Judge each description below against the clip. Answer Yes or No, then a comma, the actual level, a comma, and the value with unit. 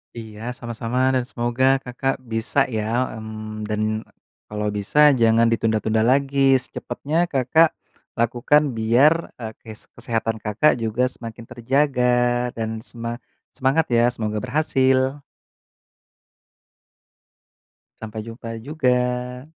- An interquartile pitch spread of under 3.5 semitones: Yes, average, 2.9 semitones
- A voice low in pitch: Yes, low, 120 Hz